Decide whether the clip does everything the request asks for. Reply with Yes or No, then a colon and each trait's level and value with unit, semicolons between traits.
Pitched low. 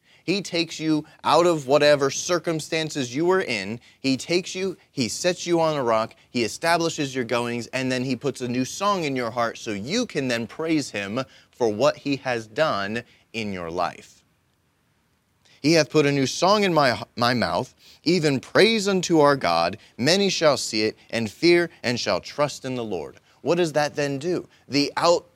No: medium, 145 Hz